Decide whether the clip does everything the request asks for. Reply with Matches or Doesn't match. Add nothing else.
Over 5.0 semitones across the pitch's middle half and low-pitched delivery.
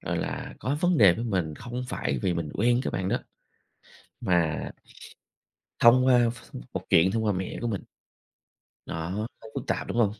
Matches